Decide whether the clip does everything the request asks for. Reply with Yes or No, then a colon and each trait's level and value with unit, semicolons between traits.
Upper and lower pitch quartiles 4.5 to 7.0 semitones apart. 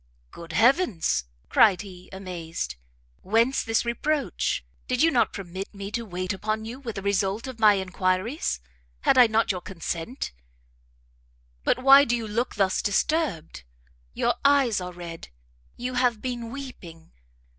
Yes: average, 5.1 semitones